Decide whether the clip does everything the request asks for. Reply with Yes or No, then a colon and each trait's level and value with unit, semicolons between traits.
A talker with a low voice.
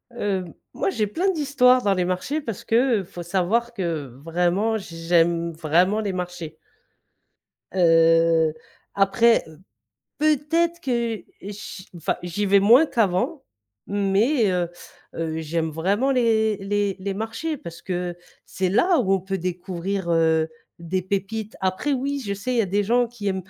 No: high, 195 Hz